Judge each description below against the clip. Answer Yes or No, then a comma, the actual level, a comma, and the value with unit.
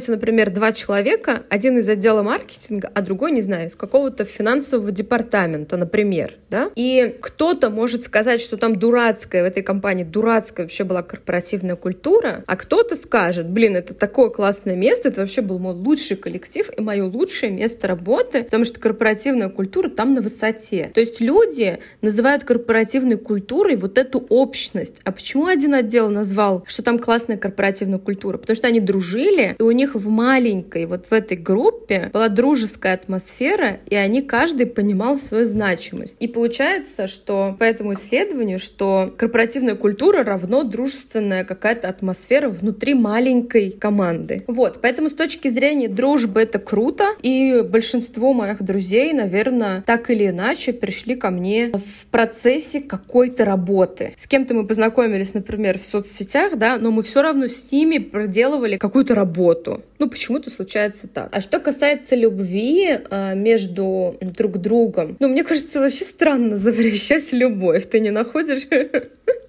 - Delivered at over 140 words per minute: Yes, average, 150 wpm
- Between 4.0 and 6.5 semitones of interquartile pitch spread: Yes, average, 4.3 semitones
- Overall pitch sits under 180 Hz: No, high, 225 Hz